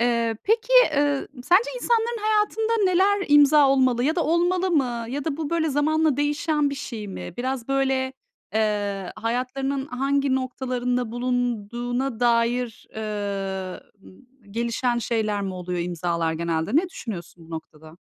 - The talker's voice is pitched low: No, very high, 250 Hz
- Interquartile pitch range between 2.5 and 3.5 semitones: No, wide, 5.4 semitones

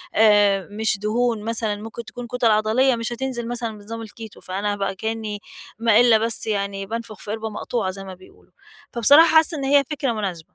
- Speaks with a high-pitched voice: Yes, high, 220 Hz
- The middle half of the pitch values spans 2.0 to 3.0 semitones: Yes, narrow, 2.4 semitones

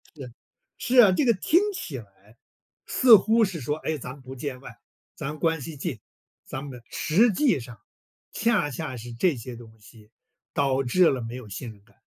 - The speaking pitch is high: No, low, 135 Hz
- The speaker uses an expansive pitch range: Yes, wide, 7.1 semitones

